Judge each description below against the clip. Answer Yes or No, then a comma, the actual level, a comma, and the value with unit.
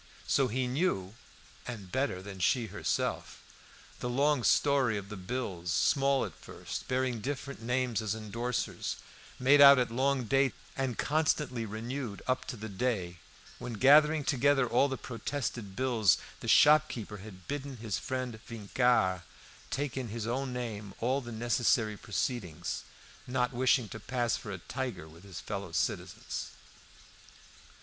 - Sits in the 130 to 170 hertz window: No, low, 120 Hz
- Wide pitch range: No, average, 4.0 semitones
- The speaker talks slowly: No, average, 145 wpm